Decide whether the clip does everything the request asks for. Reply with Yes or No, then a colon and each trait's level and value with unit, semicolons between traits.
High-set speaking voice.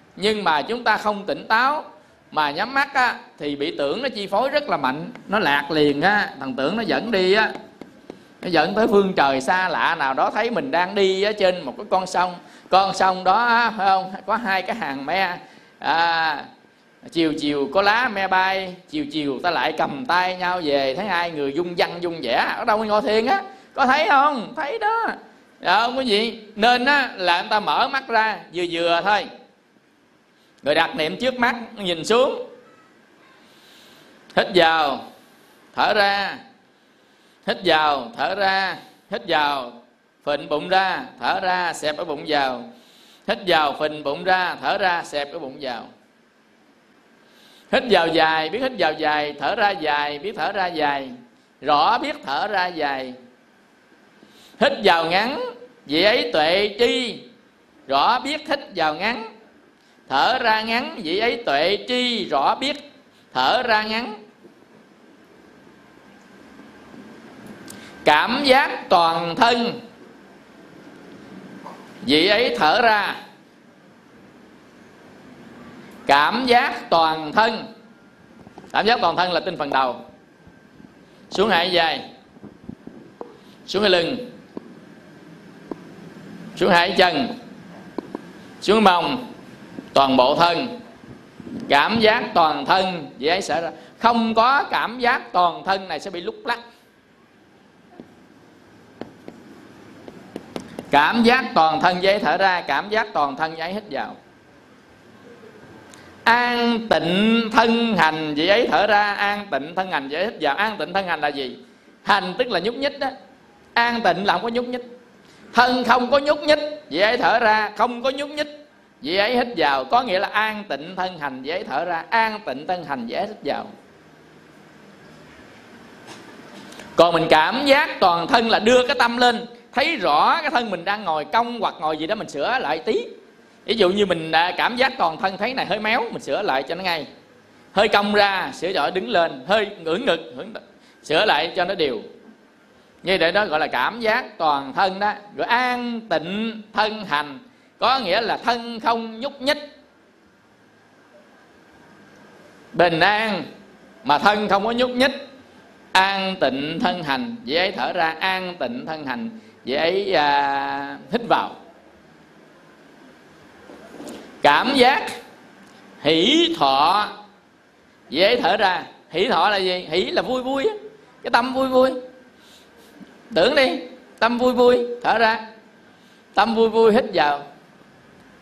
Yes: high, 210 Hz